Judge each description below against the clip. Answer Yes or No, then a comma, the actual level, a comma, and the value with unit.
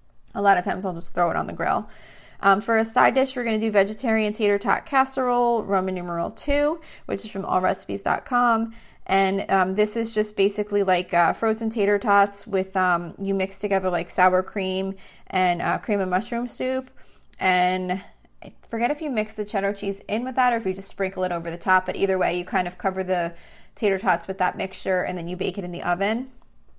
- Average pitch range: Yes, average, 3.2 semitones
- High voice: Yes, high, 195 Hz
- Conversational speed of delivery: No, fast, 215 wpm